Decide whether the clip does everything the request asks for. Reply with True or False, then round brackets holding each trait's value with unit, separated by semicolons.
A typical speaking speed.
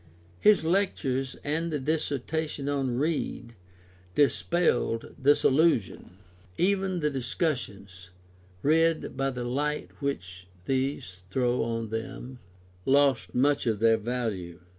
False (115 wpm)